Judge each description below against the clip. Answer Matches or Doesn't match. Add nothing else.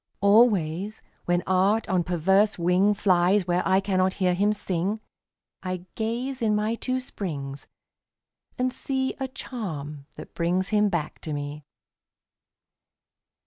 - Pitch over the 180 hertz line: Matches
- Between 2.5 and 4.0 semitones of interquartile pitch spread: Matches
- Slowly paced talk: Matches